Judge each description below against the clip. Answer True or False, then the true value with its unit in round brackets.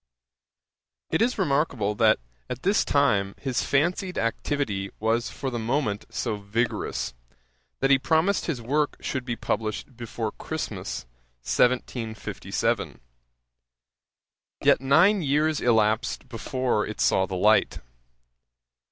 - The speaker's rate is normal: False (115 wpm)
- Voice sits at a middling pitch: False (125 Hz)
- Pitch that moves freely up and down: False (4.7 semitones)